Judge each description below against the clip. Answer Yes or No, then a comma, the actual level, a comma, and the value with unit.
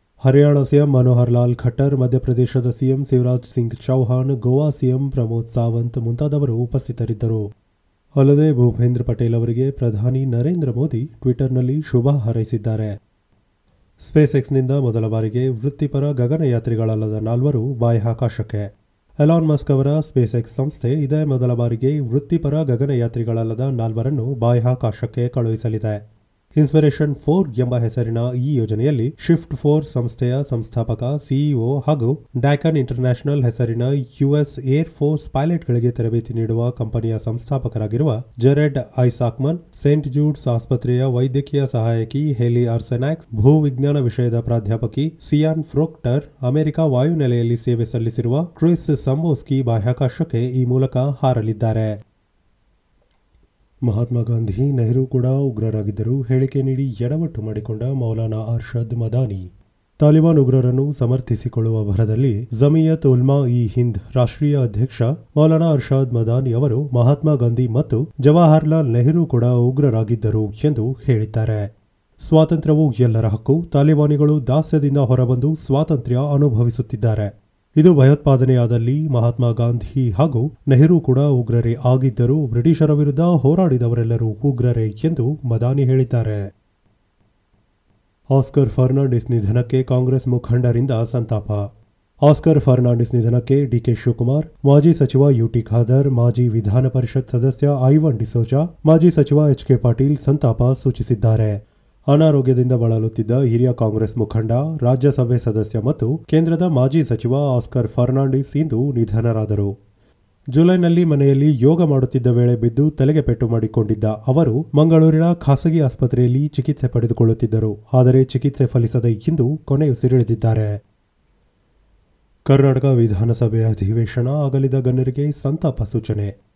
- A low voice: Yes, low, 125 Hz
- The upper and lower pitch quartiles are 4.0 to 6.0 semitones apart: No, average, 3.5 semitones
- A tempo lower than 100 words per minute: No, fast, 105 wpm